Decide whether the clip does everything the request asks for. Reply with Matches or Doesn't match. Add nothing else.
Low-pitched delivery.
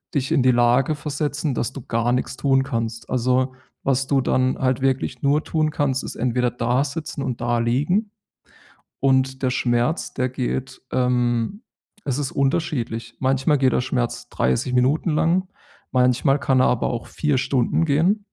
Matches